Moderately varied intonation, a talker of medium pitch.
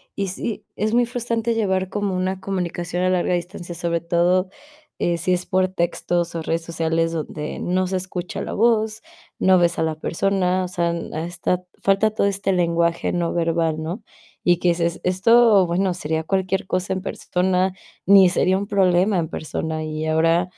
No: narrow, 2.2 semitones; medium, 180 Hz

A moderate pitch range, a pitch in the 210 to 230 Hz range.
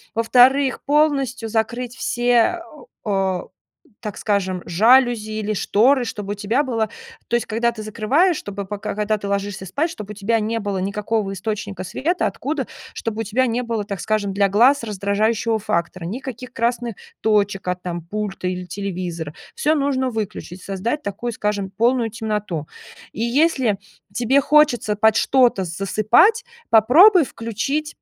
Yes: average, 3.6 semitones; high, 220 Hz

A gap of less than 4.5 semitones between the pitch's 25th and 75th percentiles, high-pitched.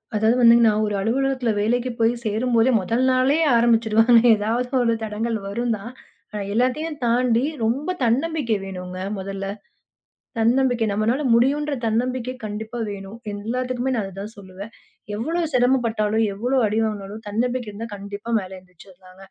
Yes: average, 3.2 semitones; high, 225 Hz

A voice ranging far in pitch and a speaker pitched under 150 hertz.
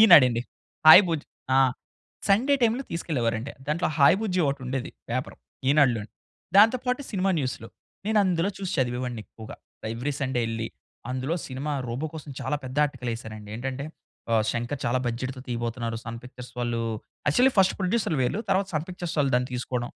Yes: wide, 6.1 semitones; low, 135 Hz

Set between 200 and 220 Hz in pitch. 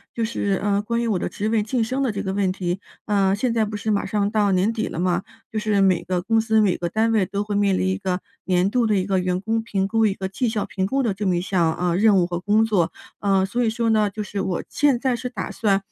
Yes: high, 205 Hz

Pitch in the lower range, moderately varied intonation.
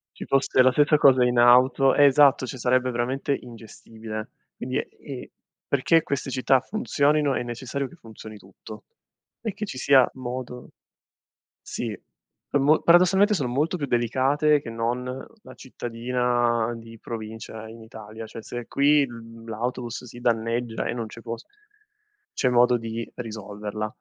Yes: low, 125 Hz; average, 3.1 semitones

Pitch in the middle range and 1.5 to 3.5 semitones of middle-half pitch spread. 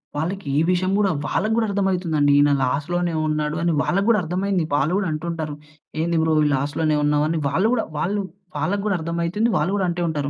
No: medium, 170 Hz; average, 4.1 semitones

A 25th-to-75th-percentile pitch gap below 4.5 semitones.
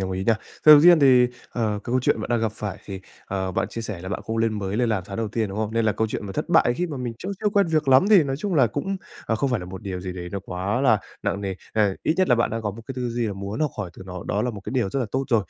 No: average, 4.8 semitones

